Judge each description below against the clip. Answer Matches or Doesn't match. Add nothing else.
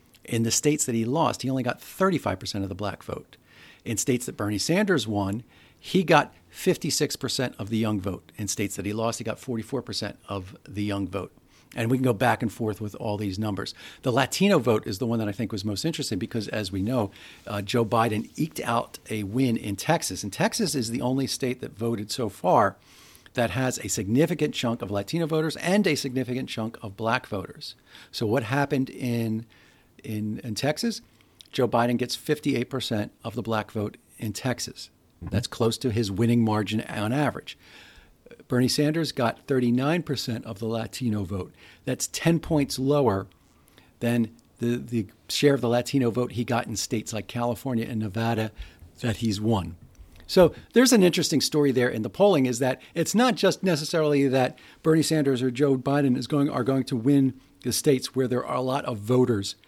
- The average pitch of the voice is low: Matches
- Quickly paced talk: Doesn't match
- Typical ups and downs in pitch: Matches